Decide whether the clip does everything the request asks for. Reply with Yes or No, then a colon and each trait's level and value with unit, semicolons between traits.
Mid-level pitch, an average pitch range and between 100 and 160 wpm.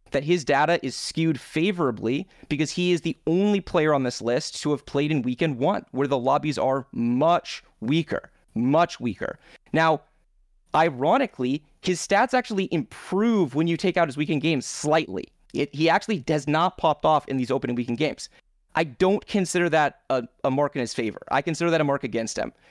No: medium, 155 Hz; average, 4.1 semitones; average, 190 wpm